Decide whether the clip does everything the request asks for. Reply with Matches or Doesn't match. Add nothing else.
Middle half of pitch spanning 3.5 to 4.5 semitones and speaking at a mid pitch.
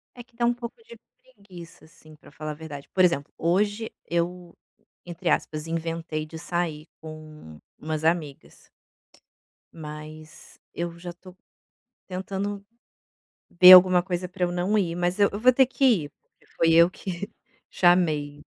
Doesn't match